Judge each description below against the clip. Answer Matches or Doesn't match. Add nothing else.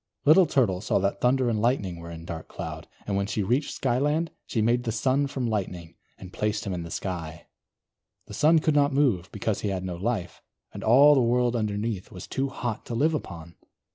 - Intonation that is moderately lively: Doesn't match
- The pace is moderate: Doesn't match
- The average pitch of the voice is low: Matches